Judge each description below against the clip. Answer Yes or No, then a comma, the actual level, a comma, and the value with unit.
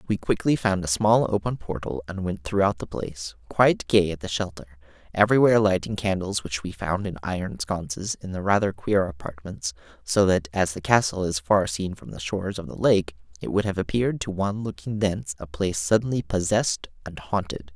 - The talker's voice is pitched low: Yes, very low, 95 Hz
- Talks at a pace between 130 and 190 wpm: No, average, 200 wpm